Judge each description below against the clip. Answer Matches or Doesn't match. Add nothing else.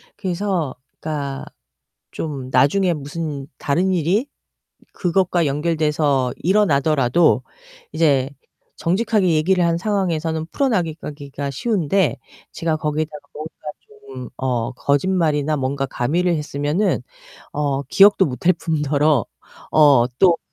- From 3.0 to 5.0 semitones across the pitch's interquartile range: Matches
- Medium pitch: Matches